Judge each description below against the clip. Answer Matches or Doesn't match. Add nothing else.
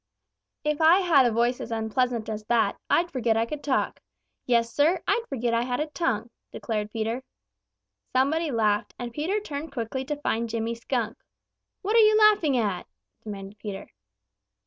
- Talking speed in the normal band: Matches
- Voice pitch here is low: Doesn't match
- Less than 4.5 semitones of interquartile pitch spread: Doesn't match